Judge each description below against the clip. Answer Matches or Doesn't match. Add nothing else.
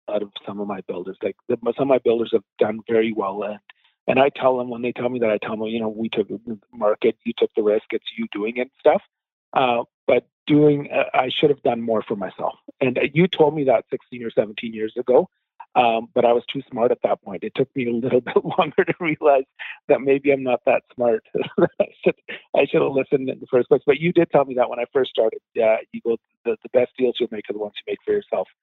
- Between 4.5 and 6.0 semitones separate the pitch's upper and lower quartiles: Matches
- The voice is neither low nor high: Doesn't match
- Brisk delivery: Matches